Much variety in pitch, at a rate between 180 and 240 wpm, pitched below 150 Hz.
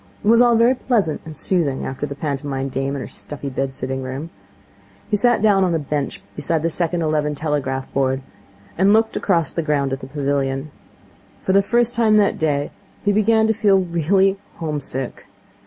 No: wide, 6.4 semitones; average, 190 wpm; medium, 155 Hz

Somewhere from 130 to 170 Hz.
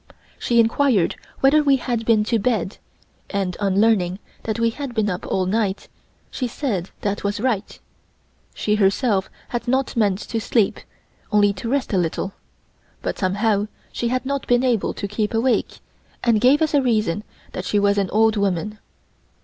No: high, 215 Hz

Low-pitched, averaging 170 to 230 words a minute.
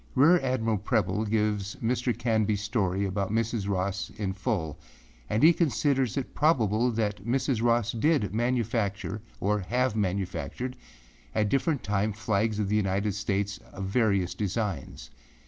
No: low, 110 Hz; average, 140 wpm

